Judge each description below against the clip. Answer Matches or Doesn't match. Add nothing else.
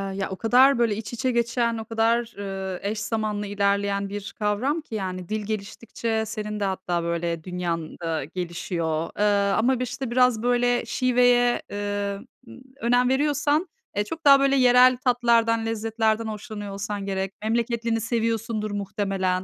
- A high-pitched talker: Matches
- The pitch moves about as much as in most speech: Matches